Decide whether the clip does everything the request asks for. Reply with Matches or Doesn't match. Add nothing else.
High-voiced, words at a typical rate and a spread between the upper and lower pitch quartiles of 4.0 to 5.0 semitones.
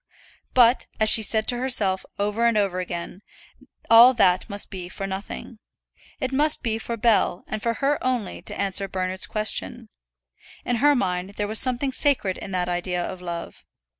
Matches